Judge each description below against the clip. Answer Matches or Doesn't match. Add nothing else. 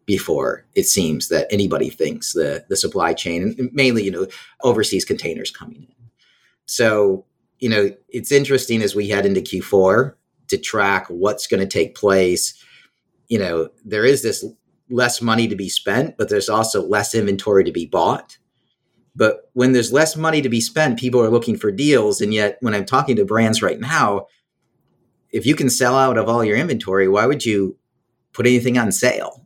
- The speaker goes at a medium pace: Matches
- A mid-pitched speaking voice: Doesn't match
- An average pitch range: Matches